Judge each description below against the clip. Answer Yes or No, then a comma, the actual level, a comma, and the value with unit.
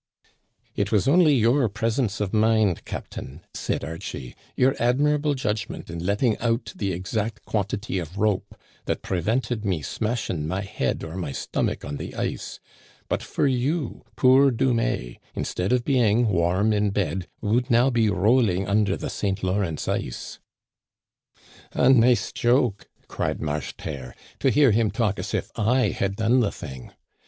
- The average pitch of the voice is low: Yes, low, 105 Hz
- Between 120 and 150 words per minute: No, average, 160 wpm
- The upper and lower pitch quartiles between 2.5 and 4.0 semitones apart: No, average, 4.5 semitones